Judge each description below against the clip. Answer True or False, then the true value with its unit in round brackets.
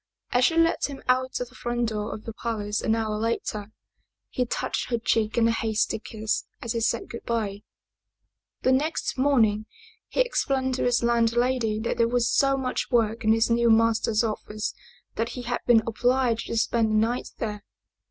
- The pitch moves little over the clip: True (2.1 semitones)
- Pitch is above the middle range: True (230 Hz)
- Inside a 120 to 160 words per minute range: False (190 wpm)